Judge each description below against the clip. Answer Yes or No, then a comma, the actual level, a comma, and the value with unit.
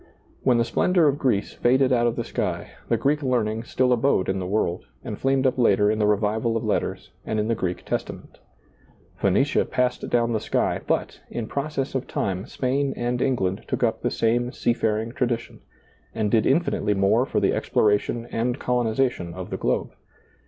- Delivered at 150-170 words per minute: No, average, 190 wpm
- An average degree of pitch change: Yes, average, 3.2 semitones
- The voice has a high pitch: No, low, 120 Hz